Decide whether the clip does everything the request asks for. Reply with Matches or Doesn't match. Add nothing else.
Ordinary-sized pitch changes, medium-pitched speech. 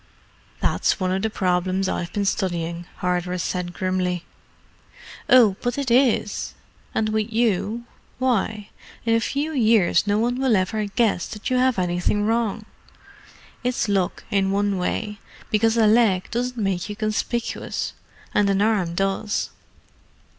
Doesn't match